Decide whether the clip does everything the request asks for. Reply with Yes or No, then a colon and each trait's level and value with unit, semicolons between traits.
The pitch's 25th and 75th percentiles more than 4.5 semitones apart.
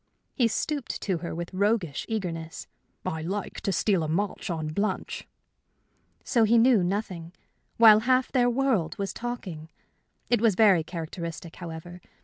Yes: average, 5.3 semitones